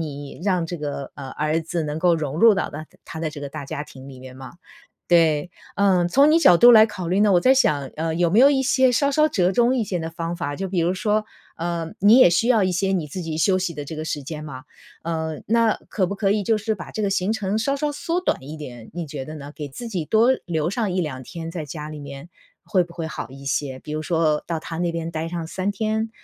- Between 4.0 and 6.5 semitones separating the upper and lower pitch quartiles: Yes, average, 5.1 semitones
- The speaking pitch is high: No, medium, 170 Hz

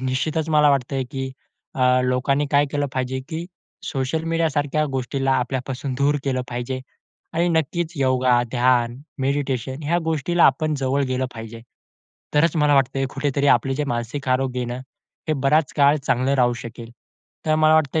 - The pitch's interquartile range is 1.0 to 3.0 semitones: Yes, average, 2.7 semitones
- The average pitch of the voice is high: No, low, 135 Hz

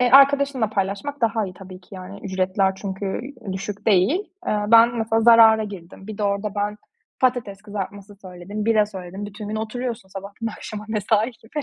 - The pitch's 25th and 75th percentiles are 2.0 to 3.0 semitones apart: Yes, average, 2.7 semitones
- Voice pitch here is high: Yes, high, 210 Hz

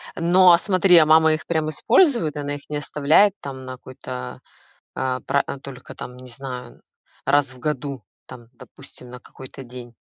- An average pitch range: Yes, average, 3.6 semitones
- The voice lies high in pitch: No, medium, 140 Hz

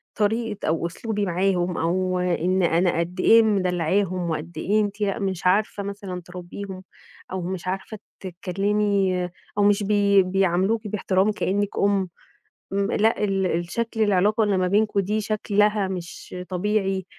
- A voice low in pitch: No, high, 195 Hz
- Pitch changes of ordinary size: No, narrow, 2.3 semitones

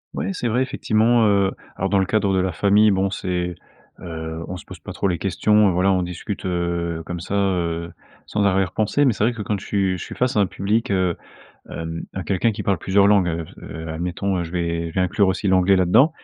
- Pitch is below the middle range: Yes, very low, 95 Hz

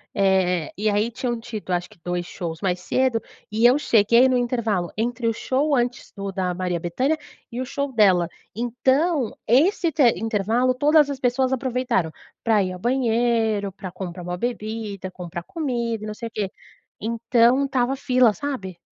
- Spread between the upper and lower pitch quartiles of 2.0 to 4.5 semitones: No, average, 4.9 semitones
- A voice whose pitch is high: Yes, high, 230 Hz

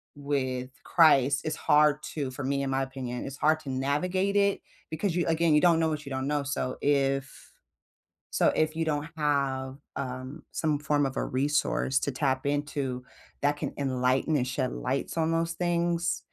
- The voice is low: No, medium, 145 Hz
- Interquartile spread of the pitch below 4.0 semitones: Yes, average, 2.9 semitones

